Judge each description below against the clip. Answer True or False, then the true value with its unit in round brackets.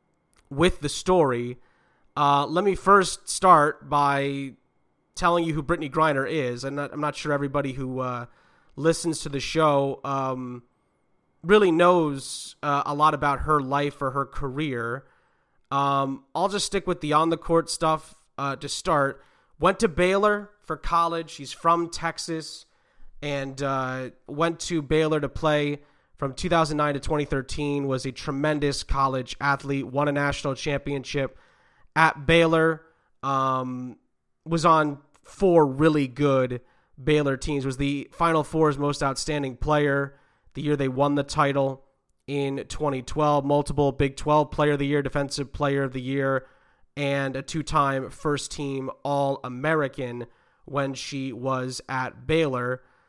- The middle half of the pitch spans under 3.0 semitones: True (2.5 semitones)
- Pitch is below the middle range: False (145 Hz)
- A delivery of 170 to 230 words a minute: False (145 wpm)